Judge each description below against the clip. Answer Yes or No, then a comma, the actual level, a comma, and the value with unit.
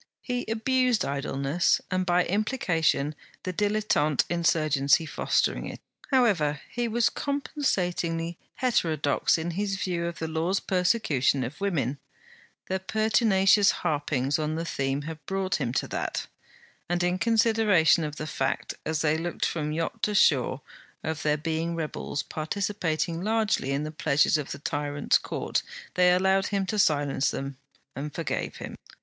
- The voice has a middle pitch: Yes, medium, 170 Hz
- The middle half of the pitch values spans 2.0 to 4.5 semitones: No, average, 4.9 semitones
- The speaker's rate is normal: Yes, average, 145 wpm